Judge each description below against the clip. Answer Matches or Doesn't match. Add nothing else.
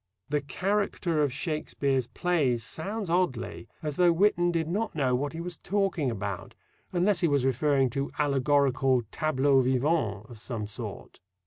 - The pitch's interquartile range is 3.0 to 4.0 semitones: Doesn't match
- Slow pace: Doesn't match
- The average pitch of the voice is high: Doesn't match